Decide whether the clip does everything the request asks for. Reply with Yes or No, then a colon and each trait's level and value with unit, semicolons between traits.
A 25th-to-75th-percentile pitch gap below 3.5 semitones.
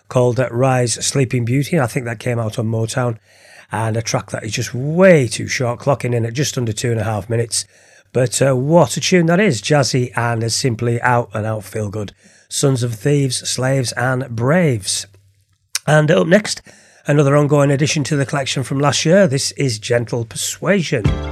No: average, 4.0 semitones